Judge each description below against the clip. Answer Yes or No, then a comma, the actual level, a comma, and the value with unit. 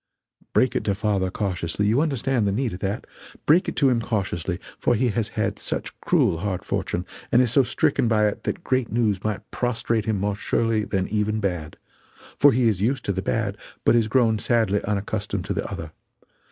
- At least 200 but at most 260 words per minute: Yes, fast, 205 wpm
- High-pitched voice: No, low, 110 Hz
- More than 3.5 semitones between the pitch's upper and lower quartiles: No, average, 3.2 semitones